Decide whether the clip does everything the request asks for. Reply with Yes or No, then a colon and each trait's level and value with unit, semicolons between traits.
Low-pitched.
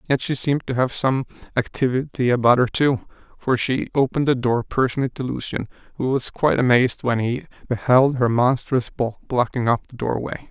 Yes: low, 125 Hz